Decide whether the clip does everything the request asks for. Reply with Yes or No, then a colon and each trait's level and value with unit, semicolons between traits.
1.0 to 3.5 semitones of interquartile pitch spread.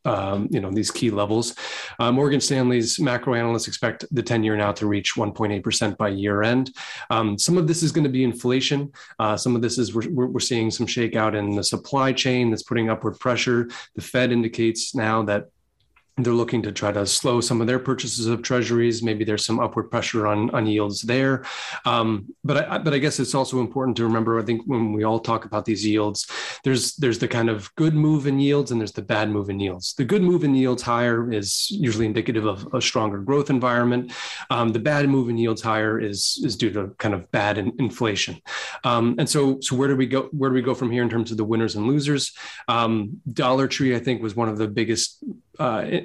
Yes: average, 3.0 semitones